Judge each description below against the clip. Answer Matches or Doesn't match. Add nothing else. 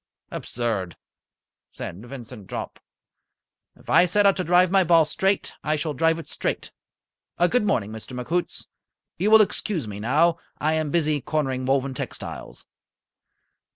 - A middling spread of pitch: Doesn't match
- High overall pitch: Doesn't match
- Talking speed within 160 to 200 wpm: Doesn't match